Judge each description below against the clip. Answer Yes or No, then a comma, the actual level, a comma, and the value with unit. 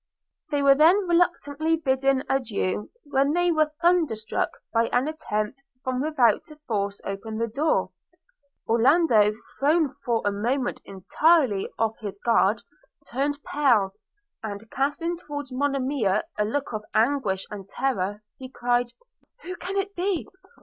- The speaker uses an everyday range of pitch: No, wide, 5.8 semitones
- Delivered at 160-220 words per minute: No, average, 140 wpm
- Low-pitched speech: No, very high, 265 Hz